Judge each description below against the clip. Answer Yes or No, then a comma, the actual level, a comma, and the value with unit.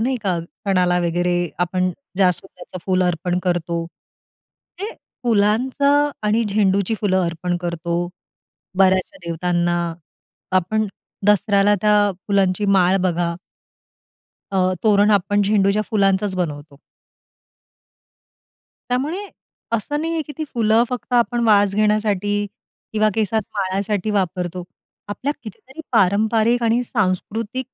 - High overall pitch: Yes, high, 200 Hz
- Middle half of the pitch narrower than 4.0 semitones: Yes, average, 3.3 semitones